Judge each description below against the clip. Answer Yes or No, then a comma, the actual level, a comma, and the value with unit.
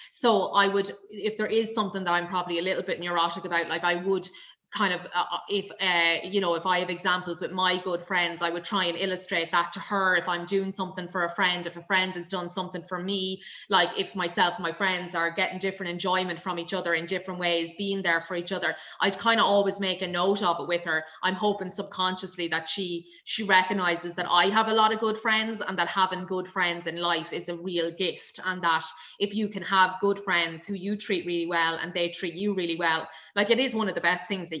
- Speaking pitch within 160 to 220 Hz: Yes, medium, 185 Hz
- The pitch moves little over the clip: Yes, narrow, 2.1 semitones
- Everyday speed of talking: No, fast, 245 wpm